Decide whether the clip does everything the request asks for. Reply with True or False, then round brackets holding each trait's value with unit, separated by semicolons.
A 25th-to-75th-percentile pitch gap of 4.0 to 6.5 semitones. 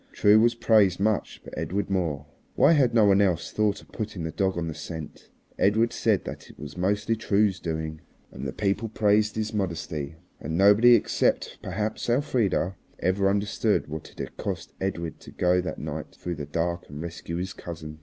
True (4.3 semitones)